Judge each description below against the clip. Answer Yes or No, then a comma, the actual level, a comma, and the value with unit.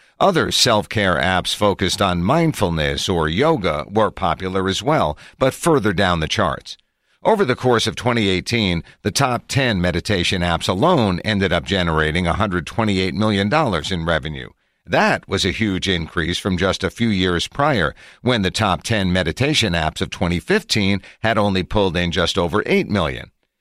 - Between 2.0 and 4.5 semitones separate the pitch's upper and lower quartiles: Yes, average, 3.4 semitones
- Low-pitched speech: Yes, very low, 95 Hz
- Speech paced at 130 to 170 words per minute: Yes, average, 160 wpm